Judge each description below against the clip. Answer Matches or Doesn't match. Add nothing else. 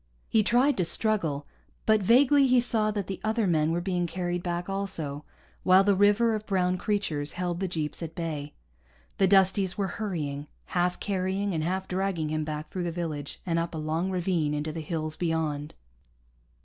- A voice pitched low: Doesn't match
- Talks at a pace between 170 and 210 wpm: Matches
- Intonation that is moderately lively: Matches